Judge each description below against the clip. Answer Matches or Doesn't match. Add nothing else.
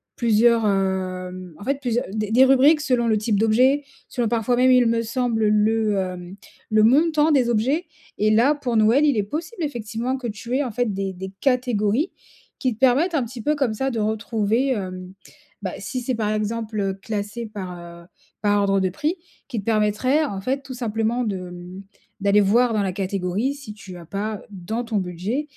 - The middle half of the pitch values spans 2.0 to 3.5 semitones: Doesn't match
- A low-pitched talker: Doesn't match